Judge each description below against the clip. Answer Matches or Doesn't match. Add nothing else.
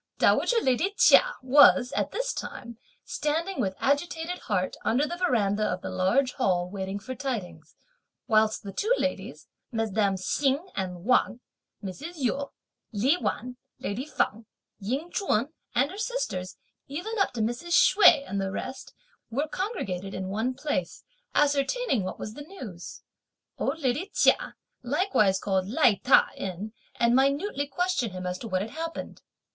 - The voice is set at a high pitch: Matches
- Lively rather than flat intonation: Matches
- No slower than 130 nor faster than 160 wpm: Matches